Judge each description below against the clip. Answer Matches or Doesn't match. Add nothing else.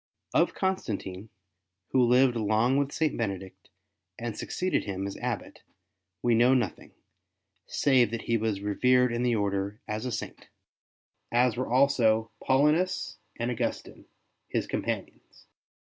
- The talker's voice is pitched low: Matches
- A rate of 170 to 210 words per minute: Doesn't match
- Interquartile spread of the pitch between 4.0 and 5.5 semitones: Doesn't match